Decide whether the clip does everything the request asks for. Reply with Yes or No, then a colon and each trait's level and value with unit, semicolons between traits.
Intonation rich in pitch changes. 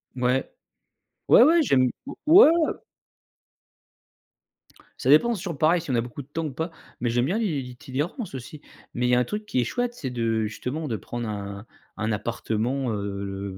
Yes: wide, 6.3 semitones